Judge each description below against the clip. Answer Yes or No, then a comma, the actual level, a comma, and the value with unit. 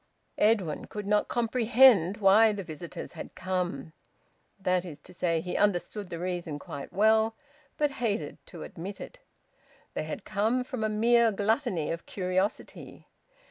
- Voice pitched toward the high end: Yes, high, 200 Hz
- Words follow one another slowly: No, average, 145 wpm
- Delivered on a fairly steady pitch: No, average, 4.0 semitones